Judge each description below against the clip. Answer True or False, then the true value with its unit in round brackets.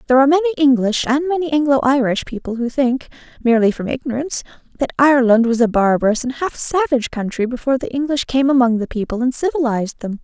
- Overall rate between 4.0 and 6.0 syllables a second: False (6.7 syllables/s)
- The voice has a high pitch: True (260 Hz)